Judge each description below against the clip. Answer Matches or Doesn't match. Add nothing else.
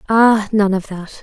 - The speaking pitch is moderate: Doesn't match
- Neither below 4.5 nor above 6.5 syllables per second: Doesn't match